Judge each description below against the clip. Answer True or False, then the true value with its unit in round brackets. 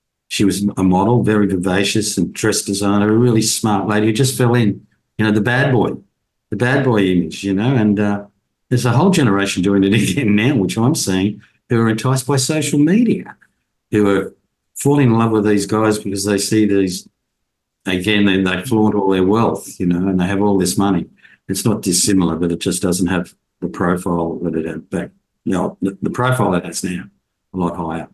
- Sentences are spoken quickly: True (210 wpm)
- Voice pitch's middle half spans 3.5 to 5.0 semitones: False (2.9 semitones)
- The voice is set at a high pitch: False (100 Hz)